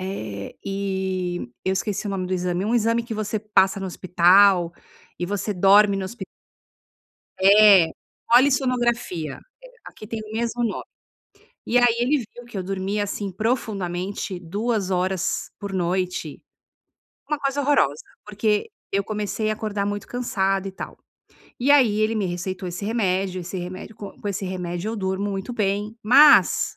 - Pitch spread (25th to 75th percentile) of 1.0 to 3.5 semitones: Yes, average, 2.9 semitones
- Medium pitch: No, high, 200 Hz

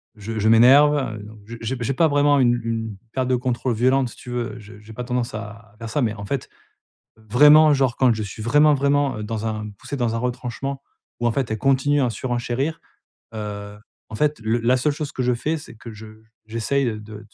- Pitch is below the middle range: Yes, low, 120 Hz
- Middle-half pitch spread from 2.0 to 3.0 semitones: No, average, 3.7 semitones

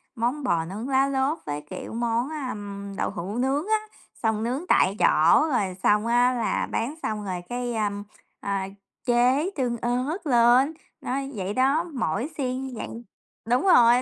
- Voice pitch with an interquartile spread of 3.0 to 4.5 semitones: Yes, average, 4.2 semitones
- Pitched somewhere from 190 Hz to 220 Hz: No, high, 240 Hz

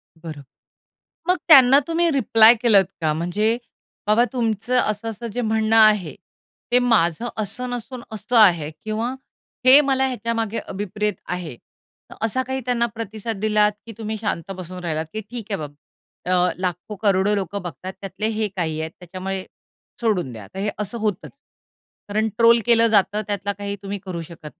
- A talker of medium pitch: No, high, 210 Hz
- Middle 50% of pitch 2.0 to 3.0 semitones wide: No, average, 3.7 semitones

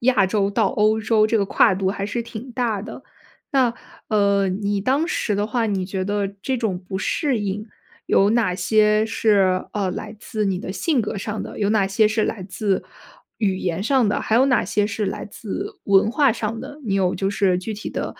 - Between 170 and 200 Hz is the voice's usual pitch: No, high, 210 Hz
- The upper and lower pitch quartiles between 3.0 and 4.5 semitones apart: No, narrow, 2.4 semitones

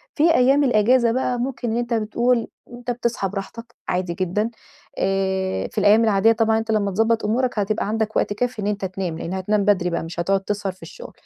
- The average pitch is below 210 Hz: No, high, 215 Hz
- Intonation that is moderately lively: Yes, average, 3.4 semitones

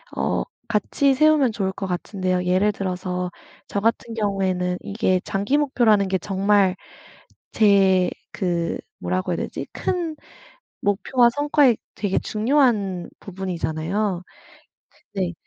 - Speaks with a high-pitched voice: Yes, high, 195 Hz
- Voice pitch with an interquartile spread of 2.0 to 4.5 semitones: Yes, average, 3.6 semitones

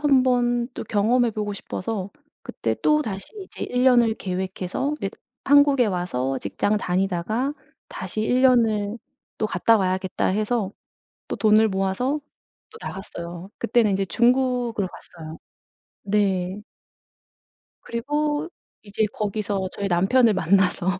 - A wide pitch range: No, average, 4.4 semitones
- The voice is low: No, high, 210 Hz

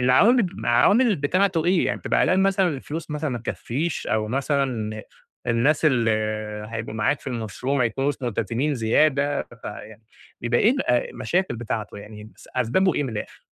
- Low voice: Yes, low, 130 Hz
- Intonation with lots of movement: Yes, wide, 5.7 semitones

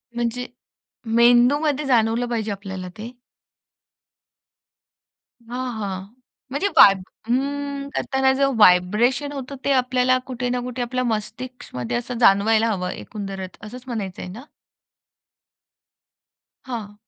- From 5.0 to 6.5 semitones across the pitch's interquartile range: No, average, 3.6 semitones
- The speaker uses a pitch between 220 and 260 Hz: Yes, high, 240 Hz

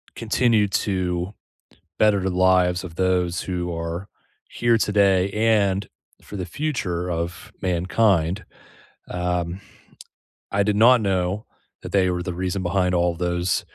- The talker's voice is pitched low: Yes, very low, 95 Hz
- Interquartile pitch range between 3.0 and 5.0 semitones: No, narrow, 2.4 semitones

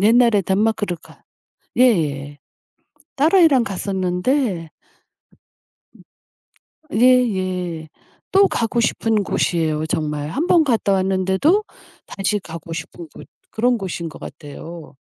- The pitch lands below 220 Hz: Yes, high, 190 Hz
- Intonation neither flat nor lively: No, wide, 6.3 semitones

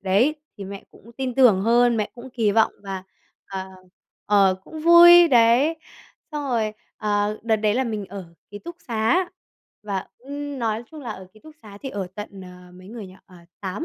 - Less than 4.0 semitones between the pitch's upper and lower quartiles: No, average, 4.7 semitones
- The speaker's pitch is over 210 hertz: Yes, high, 220 Hz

